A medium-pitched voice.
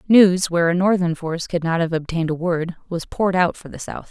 Yes: medium, 170 Hz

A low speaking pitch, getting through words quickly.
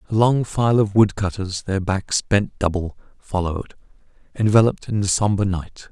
No: low, 100 Hz; average, 150 wpm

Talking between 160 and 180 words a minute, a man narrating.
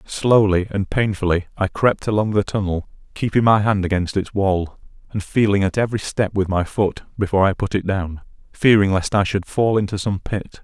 No: average, 200 wpm; male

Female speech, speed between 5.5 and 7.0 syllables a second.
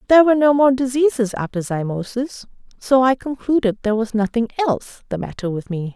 Yes: female; 6.0 syllables/s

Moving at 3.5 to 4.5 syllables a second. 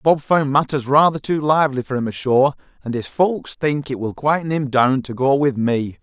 No: 5.0 syllables/s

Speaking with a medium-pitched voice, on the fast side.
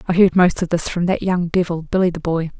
Yes: medium, 175 Hz; fast, 275 wpm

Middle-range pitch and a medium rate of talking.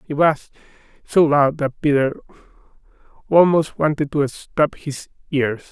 No: medium, 145 Hz; slow, 125 wpm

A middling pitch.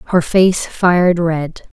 Yes: medium, 175 Hz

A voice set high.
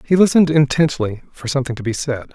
No: medium, 140 Hz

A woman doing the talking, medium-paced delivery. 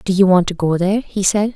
No: female; fast, 310 wpm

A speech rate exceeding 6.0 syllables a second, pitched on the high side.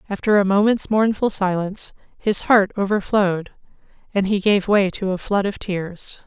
No: 4.9 syllables/s; high, 200 Hz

